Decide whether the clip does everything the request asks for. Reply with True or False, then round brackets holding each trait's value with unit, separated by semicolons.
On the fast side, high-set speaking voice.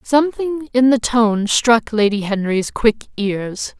False (140 wpm; 230 Hz)